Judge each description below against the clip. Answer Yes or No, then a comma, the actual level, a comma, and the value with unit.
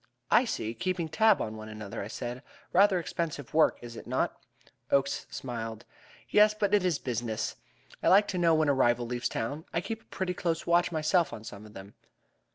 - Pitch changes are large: Yes, wide, 7.8 semitones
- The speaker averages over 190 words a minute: Yes, average, 200 wpm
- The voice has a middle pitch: Yes, medium, 145 Hz